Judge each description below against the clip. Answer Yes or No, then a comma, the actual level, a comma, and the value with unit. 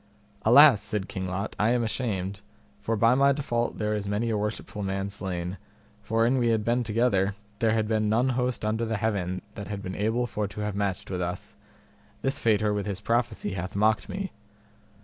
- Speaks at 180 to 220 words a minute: Yes, average, 200 wpm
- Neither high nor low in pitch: No, low, 105 Hz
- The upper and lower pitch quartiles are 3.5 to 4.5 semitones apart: No, average, 2.7 semitones